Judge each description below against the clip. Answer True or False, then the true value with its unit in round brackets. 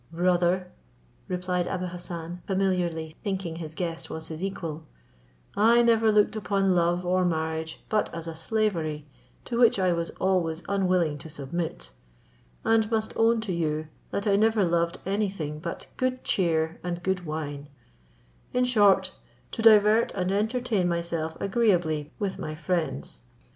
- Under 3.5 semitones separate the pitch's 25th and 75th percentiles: False (3.8 semitones)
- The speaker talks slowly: False (150 wpm)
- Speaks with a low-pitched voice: False (180 Hz)